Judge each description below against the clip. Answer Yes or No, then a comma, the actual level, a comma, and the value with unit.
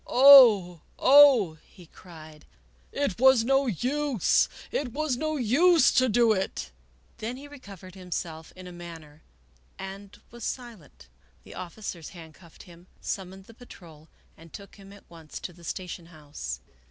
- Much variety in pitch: Yes, wide, 6.8 semitones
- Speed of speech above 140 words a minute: Yes, average, 160 wpm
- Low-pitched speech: No, high, 190 Hz